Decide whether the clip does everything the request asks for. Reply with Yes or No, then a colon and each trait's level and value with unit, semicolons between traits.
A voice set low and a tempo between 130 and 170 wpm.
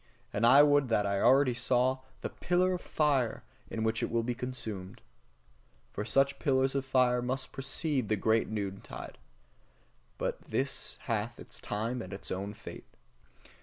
Yes: low, 125 Hz; average, 160 wpm